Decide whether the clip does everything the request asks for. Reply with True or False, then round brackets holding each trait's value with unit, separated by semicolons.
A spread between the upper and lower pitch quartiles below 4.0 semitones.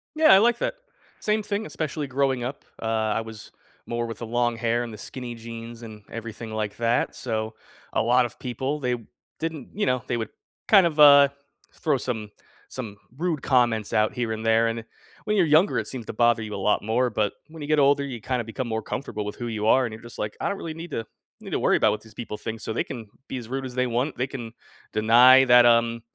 True (3.4 semitones)